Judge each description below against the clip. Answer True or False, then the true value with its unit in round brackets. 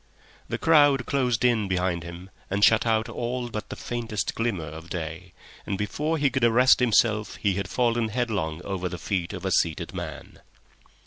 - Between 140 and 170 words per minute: False (180 wpm)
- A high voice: False (110 Hz)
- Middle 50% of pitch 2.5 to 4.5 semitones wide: False (4.9 semitones)